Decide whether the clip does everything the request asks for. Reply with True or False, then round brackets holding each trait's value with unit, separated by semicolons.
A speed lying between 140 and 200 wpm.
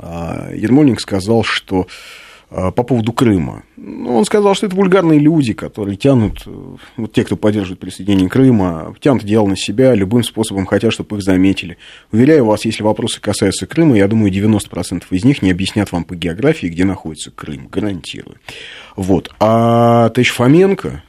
True (155 wpm)